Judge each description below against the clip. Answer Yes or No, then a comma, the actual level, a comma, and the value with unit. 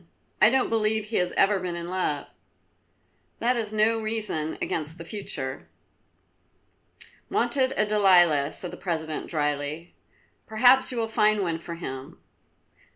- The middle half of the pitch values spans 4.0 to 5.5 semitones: Yes, average, 5.2 semitones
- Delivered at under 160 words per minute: Yes, average, 140 wpm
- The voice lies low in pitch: No, high, 190 Hz